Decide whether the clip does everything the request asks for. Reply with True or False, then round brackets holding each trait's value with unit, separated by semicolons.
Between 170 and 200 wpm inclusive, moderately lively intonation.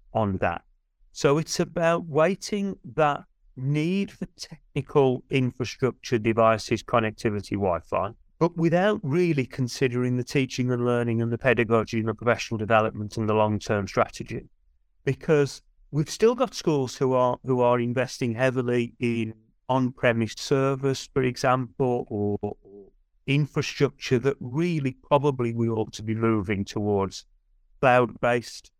False (135 wpm; 4.1 semitones)